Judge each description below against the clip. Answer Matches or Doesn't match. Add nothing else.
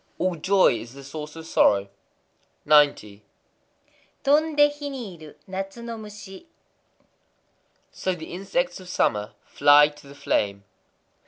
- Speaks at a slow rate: Matches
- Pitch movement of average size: Doesn't match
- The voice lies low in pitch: Doesn't match